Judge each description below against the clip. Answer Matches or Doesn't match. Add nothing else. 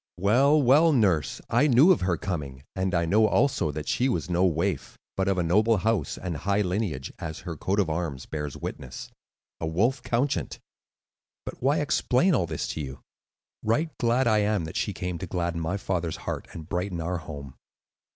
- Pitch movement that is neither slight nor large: Doesn't match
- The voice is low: Matches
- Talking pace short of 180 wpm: Doesn't match